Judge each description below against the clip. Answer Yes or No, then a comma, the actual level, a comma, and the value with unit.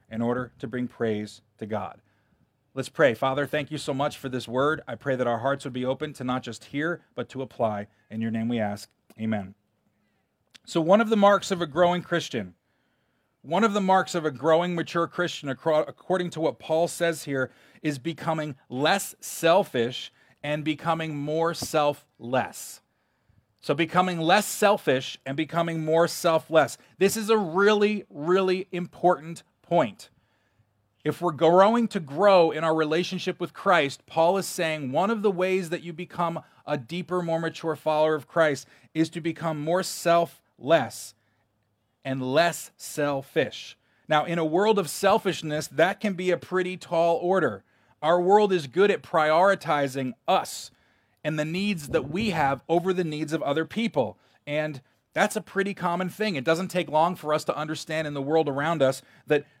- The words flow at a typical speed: Yes, average, 175 wpm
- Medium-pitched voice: Yes, medium, 160 Hz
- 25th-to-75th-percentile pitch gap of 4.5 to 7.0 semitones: Yes, average, 4.8 semitones